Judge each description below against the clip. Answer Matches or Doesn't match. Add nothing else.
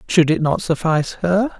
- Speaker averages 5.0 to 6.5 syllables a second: Matches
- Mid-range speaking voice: Matches